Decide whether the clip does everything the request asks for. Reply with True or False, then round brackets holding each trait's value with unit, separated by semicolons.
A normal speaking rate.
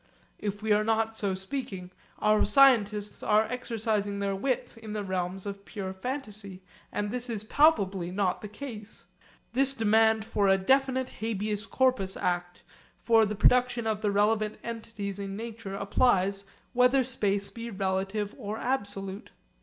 True (150 wpm)